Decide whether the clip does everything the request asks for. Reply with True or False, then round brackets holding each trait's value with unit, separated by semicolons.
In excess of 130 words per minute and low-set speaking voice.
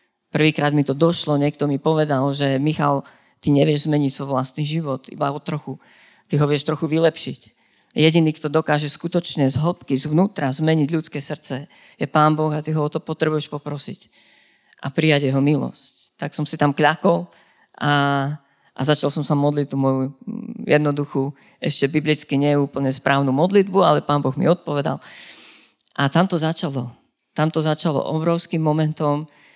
False (160 wpm; 150 Hz)